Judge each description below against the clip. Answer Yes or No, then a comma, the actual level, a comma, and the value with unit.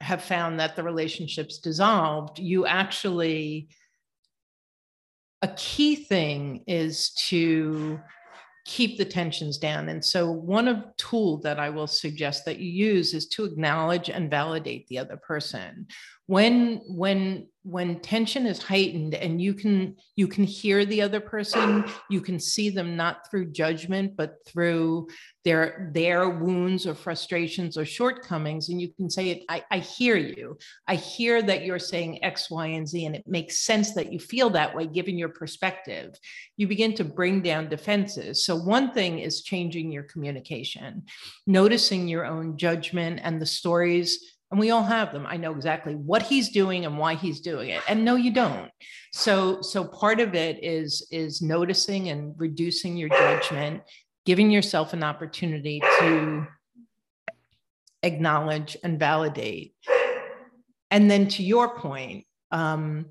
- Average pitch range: Yes, average, 3.9 semitones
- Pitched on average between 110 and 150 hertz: No, medium, 175 Hz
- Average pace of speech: Yes, average, 155 wpm